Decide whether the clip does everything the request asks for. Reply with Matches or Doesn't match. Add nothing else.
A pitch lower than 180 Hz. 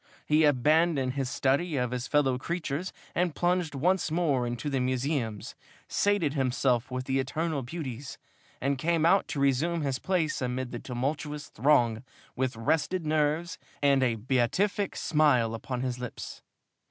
Matches